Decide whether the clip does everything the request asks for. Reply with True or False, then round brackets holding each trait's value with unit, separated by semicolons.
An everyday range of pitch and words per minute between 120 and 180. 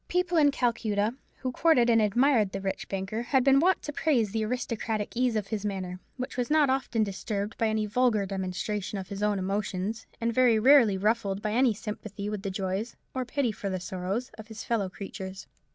False (3.8 semitones; 200 wpm)